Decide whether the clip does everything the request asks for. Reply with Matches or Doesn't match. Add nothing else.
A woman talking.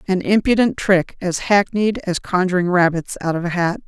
Matches